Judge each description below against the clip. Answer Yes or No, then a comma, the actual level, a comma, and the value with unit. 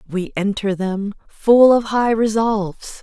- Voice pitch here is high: Yes, high, 210 Hz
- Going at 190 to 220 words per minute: No, average, 140 wpm